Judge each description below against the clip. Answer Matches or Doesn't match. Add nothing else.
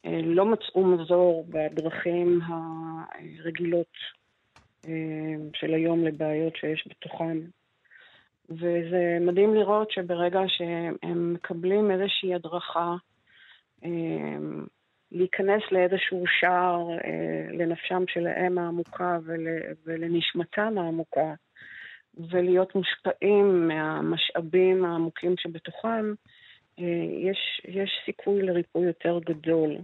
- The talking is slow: Matches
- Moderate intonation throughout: Doesn't match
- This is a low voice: Doesn't match